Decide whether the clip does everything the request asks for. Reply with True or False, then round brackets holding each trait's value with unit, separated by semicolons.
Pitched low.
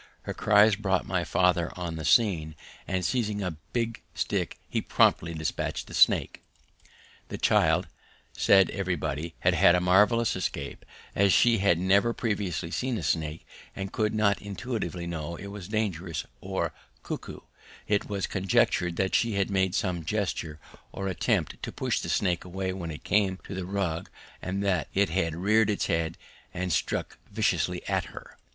True (95 Hz)